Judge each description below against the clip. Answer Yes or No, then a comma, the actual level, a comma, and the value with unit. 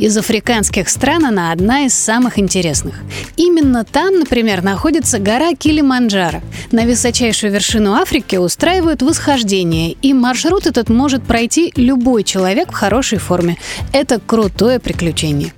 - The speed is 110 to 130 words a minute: Yes, average, 125 wpm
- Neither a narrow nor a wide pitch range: No, wide, 6.1 semitones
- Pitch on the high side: Yes, high, 235 Hz